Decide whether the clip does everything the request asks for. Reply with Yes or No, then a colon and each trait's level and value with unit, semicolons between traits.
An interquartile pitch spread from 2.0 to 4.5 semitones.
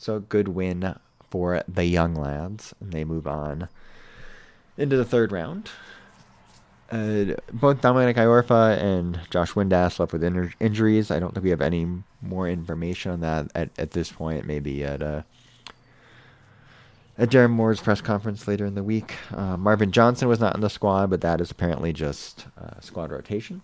No: average, 5.0 semitones